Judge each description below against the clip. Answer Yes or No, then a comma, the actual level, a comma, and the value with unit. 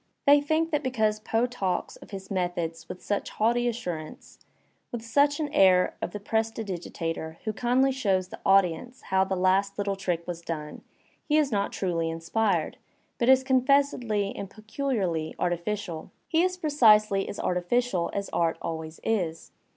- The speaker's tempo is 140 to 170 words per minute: Yes, average, 165 wpm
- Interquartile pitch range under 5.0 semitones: No, wide, 5.6 semitones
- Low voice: No, high, 200 Hz